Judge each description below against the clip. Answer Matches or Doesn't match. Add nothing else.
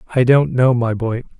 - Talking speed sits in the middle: Doesn't match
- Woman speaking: Doesn't match